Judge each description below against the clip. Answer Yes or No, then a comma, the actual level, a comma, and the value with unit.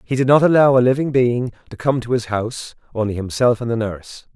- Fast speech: Yes, fast, 235 wpm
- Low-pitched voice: Yes, low, 120 Hz